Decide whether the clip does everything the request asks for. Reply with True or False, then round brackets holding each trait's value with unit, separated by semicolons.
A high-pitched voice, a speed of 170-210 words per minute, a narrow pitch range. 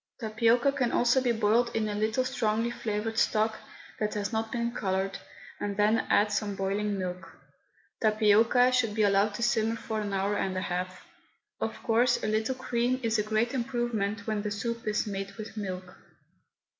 True (215 Hz; 180 wpm; 2.3 semitones)